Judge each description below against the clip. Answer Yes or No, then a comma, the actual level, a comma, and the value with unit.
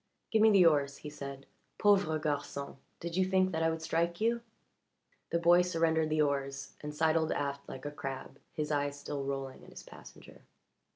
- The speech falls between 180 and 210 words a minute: Yes, average, 185 wpm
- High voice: No, medium, 155 Hz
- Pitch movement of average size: Yes, average, 3.2 semitones